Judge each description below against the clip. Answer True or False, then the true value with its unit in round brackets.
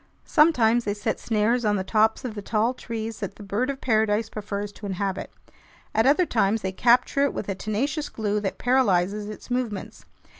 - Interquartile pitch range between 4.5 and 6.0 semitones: False (3.0 semitones)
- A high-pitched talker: True (220 Hz)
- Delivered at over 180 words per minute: True (190 wpm)